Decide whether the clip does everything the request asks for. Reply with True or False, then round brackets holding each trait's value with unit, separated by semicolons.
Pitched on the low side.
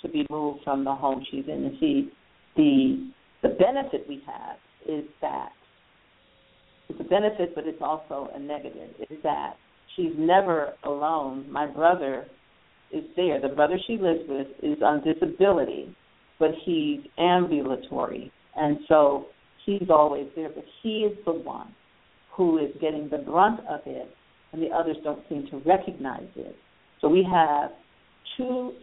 False (160 Hz)